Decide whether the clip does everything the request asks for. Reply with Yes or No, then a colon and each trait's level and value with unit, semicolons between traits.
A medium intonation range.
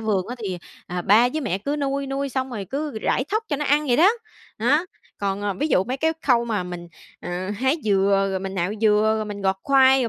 No: wide, 5.9 semitones